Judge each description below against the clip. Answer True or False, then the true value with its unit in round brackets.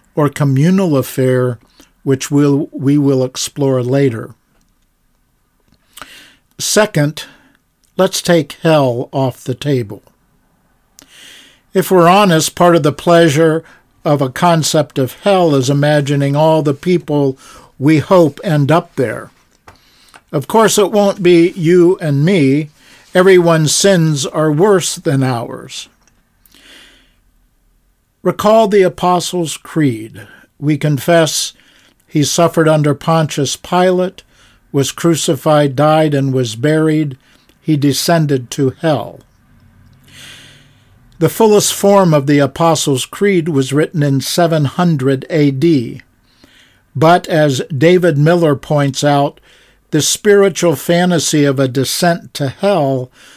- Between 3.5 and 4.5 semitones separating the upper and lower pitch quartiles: True (4.0 semitones)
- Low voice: False (150 Hz)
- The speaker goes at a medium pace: False (110 wpm)